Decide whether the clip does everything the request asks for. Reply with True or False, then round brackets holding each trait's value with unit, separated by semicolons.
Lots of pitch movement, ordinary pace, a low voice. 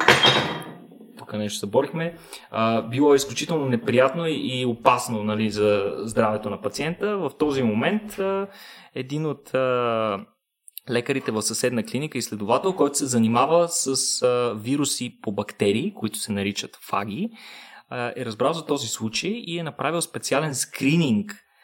True (5.9 semitones; 125 wpm; 130 Hz)